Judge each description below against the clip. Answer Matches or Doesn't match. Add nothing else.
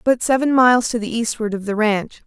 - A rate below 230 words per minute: Doesn't match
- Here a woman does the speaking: Matches